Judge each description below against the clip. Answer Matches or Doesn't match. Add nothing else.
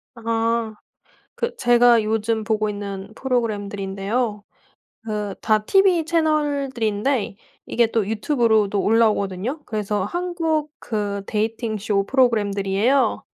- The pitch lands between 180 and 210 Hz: Doesn't match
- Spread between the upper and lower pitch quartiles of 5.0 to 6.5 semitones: Doesn't match